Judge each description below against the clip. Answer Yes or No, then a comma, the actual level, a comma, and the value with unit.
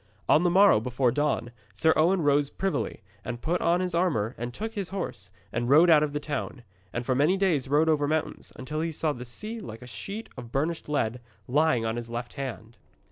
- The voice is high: No, medium, 145 Hz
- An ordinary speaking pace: No, fast, 215 wpm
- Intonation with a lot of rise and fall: Yes, wide, 5.7 semitones